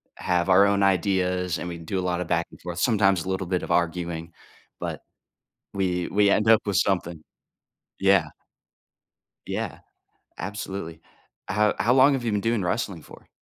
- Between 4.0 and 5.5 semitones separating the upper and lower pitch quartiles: No, narrow, 2.5 semitones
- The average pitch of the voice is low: Yes, very low, 95 Hz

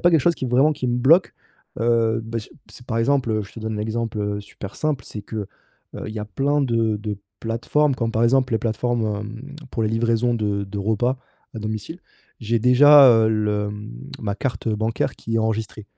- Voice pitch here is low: Yes, low, 115 Hz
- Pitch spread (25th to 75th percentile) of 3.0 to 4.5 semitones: No, narrow, 2.6 semitones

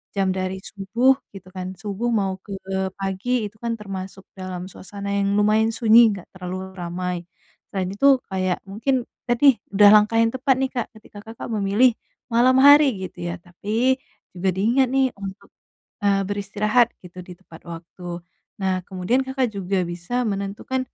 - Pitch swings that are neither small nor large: Yes, average, 4.2 semitones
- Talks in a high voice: Yes, high, 200 Hz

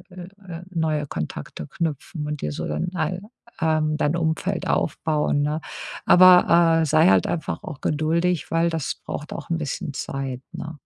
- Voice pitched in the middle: Yes, medium, 160 Hz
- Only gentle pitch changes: Yes, narrow, 2.3 semitones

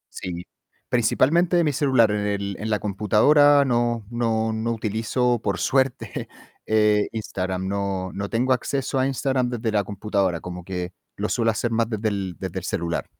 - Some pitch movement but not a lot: Yes, average, 3.7 semitones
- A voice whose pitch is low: Yes, low, 110 Hz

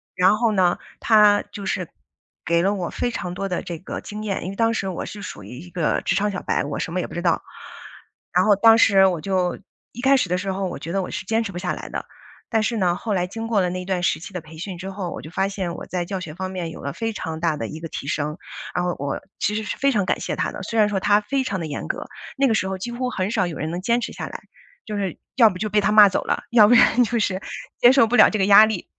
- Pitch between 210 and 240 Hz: No, high, 190 Hz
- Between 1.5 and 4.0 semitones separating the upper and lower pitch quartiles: Yes, average, 3.3 semitones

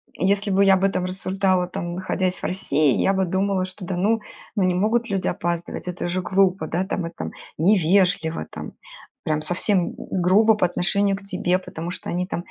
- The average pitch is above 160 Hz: Yes, medium, 185 Hz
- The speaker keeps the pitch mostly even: Yes, narrow, 1.8 semitones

